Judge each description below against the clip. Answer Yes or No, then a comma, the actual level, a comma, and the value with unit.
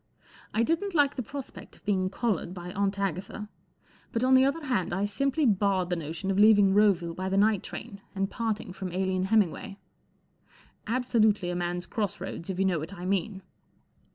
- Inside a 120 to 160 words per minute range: No, average, 190 wpm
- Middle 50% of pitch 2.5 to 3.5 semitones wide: Yes, average, 3.1 semitones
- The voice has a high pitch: Yes, high, 195 Hz